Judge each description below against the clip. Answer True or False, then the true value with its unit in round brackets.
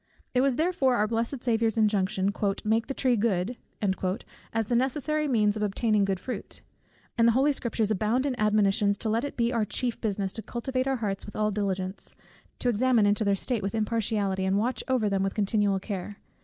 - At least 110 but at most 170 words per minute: False (195 wpm)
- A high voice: True (220 Hz)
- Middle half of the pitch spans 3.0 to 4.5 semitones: True (3.4 semitones)